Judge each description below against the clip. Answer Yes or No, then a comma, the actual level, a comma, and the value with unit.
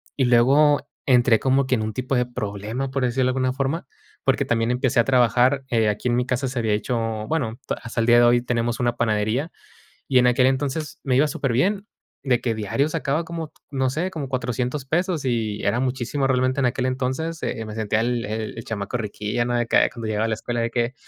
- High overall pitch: No, low, 125 Hz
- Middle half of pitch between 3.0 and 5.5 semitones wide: No, narrow, 2.6 semitones